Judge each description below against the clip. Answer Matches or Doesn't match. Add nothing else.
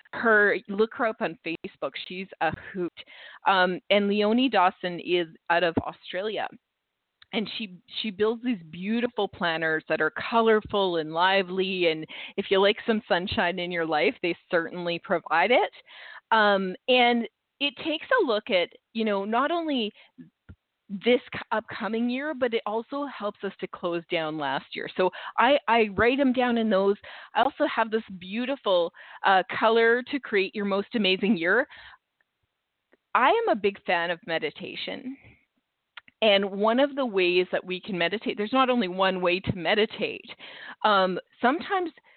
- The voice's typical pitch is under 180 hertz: Doesn't match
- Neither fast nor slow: Matches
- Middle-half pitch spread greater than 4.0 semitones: Matches